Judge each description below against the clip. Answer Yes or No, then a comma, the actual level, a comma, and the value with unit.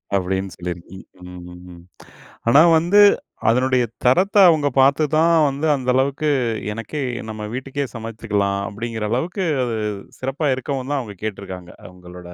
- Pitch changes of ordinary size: No, wide, 6.2 semitones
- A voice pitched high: No, low, 120 Hz